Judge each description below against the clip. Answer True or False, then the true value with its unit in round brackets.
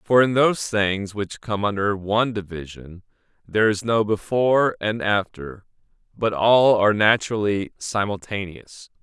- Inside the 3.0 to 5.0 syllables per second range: True (4.6 syllables/s)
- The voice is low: True (105 Hz)